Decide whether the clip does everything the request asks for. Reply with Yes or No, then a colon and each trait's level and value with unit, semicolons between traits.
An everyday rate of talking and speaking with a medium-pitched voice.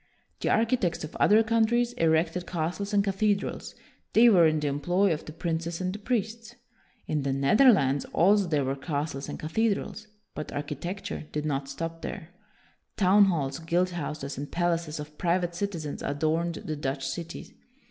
Yes: average, 160 wpm; medium, 170 Hz